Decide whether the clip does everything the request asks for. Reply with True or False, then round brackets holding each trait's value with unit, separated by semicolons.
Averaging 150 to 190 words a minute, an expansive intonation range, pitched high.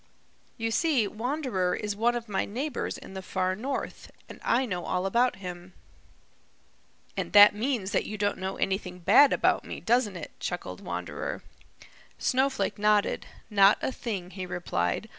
False (160 wpm; 4.3 semitones; 205 Hz)